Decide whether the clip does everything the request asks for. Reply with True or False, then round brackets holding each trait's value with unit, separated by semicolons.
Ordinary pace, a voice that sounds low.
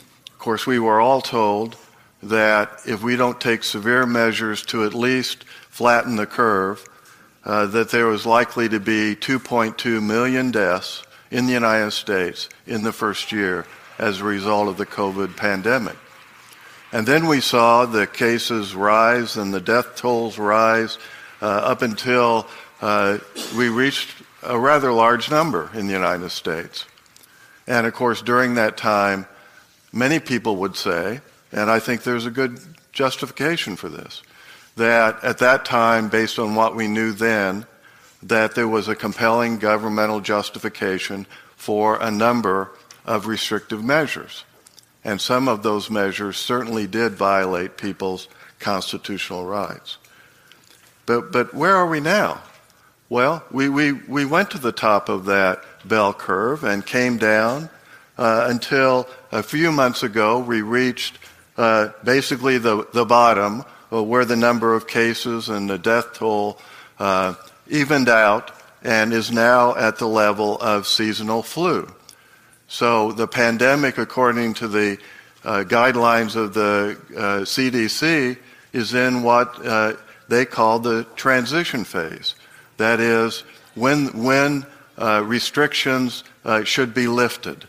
True (145 wpm; 115 Hz)